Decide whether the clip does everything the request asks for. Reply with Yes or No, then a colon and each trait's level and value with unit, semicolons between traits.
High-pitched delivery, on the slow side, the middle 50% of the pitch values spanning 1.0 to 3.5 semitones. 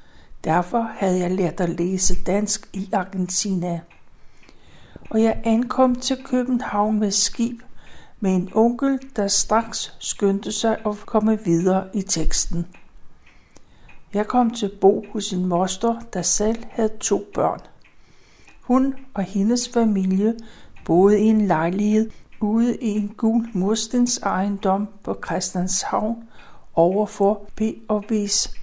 Yes: high, 210 Hz; slow, 125 wpm; average, 3.1 semitones